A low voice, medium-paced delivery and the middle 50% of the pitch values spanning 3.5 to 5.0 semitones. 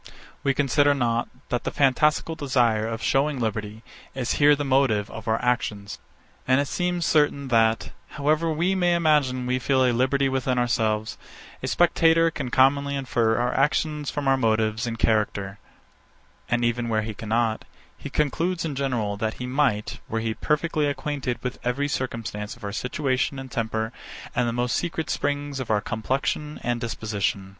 Yes: low, 125 Hz; average, 170 wpm; average, 4.2 semitones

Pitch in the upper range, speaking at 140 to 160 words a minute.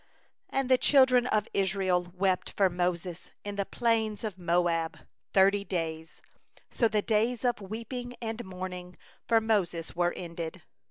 Yes: high, 195 Hz; average, 150 wpm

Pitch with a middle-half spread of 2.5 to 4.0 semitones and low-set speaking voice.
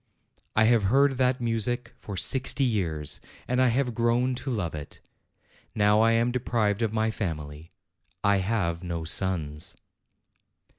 No: wide, 5.6 semitones; low, 110 Hz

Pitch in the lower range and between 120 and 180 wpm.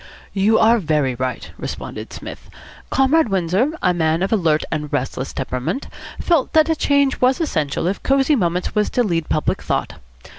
No: high, 190 Hz; average, 170 wpm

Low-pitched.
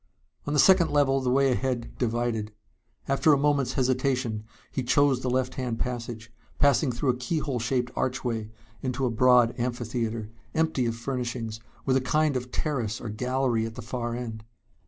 Yes: low, 125 Hz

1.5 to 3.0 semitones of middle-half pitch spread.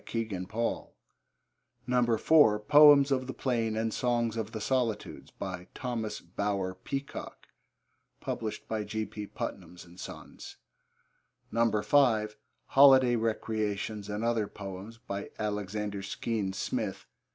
Yes: narrow, 2.5 semitones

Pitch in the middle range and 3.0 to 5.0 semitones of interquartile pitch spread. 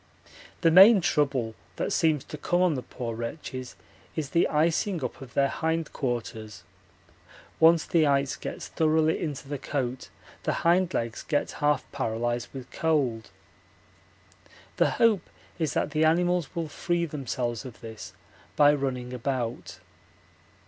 Yes: medium, 145 Hz; average, 4.6 semitones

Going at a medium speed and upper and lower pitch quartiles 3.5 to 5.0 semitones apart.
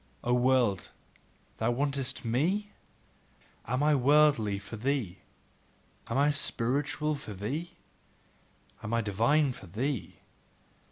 No: slow, 110 wpm; average, 4.4 semitones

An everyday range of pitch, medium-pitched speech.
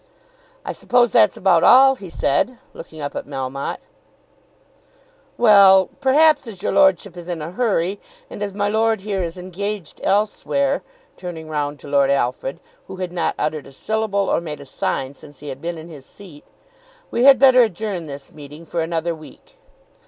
No: wide, 6.0 semitones; medium, 180 Hz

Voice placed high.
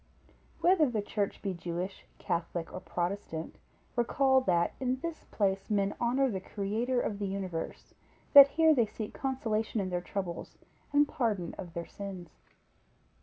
Yes: high, 205 Hz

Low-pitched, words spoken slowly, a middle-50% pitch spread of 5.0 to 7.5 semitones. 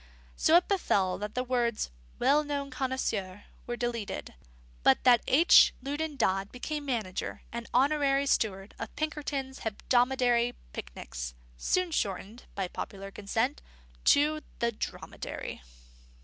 No: high, 245 Hz; slow, 120 wpm; wide, 5.5 semitones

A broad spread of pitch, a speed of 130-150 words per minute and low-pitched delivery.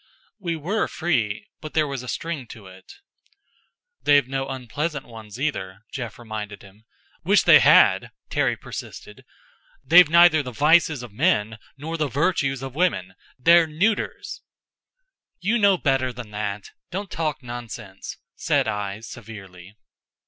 Yes: wide, 6.9 semitones; average, 140 wpm; low, 130 Hz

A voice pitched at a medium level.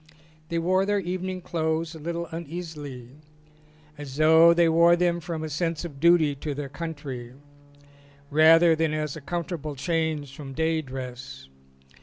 Yes: medium, 160 Hz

